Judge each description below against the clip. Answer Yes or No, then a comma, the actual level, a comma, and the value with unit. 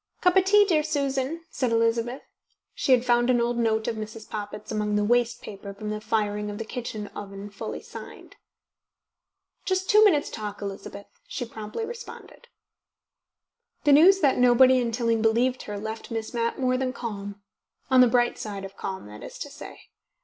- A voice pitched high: Yes, high, 230 Hz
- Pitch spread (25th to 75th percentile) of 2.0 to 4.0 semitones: Yes, average, 3.6 semitones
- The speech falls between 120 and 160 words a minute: No, average, 180 wpm